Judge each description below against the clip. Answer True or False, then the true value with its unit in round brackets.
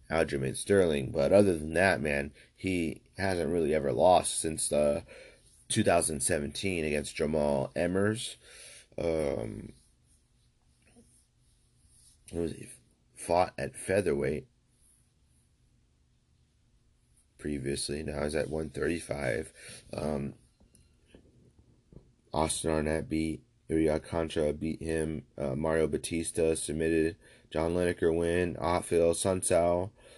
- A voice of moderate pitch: False (80 Hz)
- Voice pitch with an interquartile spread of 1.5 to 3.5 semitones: True (2.4 semitones)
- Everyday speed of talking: False (95 wpm)